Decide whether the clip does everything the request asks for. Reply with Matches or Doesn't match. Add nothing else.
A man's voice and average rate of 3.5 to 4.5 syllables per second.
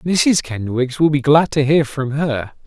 Matches